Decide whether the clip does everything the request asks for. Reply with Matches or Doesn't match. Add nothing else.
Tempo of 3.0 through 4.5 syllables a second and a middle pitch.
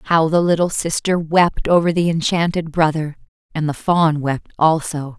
Matches